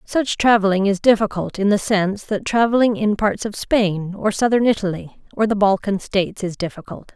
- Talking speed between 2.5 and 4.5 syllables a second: No, 5.2 syllables/s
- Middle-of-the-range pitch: No, high, 205 Hz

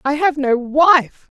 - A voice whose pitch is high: Yes, very high, 285 Hz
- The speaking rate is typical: Yes, average, 170 wpm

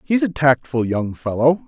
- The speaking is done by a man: Yes, male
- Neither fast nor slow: Yes, average, 180 wpm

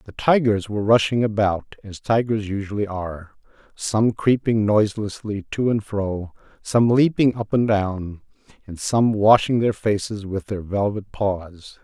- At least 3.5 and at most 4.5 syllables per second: Yes, 4.3 syllables/s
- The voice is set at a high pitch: No, low, 105 Hz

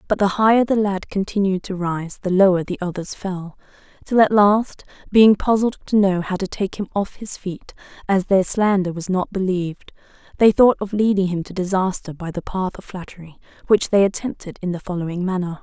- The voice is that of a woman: Yes, female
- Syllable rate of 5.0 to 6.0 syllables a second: Yes, 5.3 syllables/s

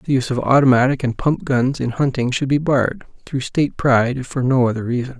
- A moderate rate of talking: No, fast, 220 wpm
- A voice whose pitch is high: No, low, 130 Hz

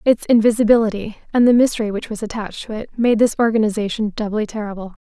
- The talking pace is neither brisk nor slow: Yes, average, 180 wpm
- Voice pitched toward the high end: Yes, high, 220 Hz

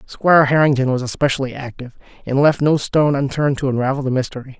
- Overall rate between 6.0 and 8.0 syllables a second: Yes, 6.9 syllables/s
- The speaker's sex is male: Yes, male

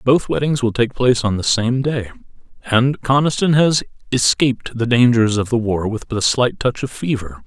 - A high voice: No, low, 120 Hz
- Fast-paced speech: No, average, 195 wpm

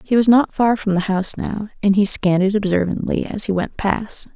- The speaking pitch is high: Yes, high, 205 Hz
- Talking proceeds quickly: Yes, fast, 235 wpm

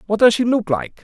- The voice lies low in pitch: No, high, 210 Hz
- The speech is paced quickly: Yes, fast, 290 wpm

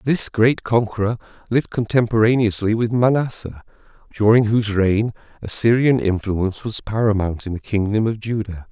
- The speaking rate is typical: No, slow, 130 wpm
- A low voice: Yes, low, 110 Hz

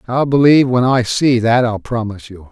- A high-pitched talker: No, low, 120 Hz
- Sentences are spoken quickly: Yes, fast, 215 wpm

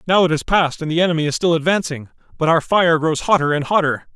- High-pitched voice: No, medium, 165 Hz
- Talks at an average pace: No, fast, 245 wpm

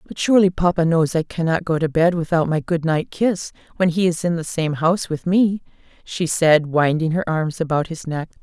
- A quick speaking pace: Yes, fast, 220 wpm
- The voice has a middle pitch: Yes, medium, 165 Hz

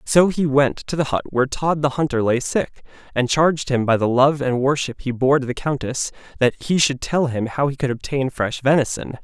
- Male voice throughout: Yes, male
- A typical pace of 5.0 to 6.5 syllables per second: Yes, 5.3 syllables/s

